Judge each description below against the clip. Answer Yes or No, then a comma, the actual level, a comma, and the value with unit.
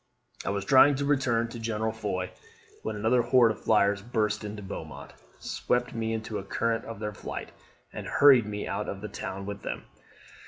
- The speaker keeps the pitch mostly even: Yes, narrow, 2.2 semitones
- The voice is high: No, low, 110 Hz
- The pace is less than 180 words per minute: No, average, 190 wpm